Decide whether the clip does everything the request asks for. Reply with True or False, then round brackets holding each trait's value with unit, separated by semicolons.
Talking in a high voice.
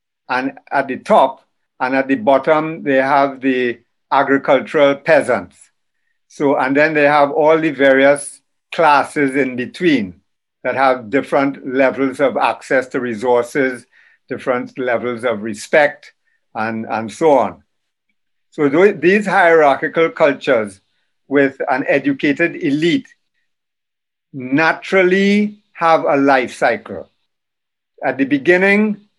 False (140 Hz)